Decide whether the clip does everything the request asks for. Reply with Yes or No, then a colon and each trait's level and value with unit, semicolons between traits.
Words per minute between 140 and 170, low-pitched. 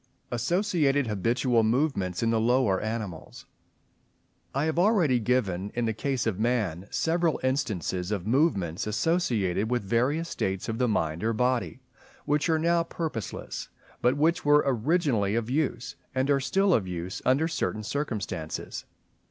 Yes: average, 145 wpm; low, 120 Hz